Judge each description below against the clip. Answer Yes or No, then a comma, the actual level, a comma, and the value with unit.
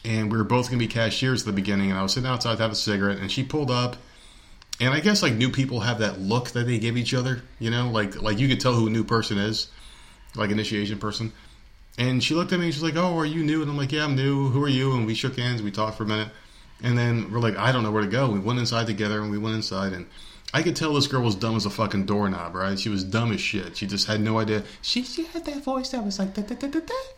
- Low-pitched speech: Yes, low, 115 Hz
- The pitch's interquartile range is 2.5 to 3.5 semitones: No, average, 4.0 semitones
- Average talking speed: No, fast, 305 wpm